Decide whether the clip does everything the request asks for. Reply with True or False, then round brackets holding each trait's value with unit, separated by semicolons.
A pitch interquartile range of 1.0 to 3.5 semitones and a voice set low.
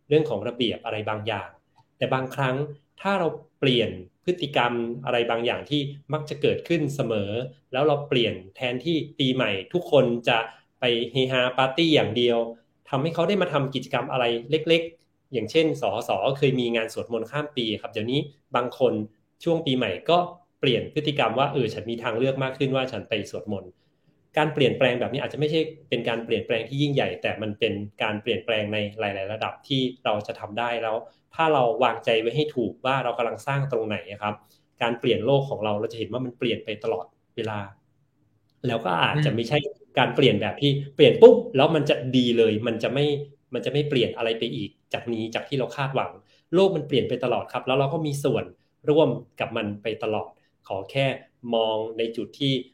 False (4.3 semitones; 125 Hz)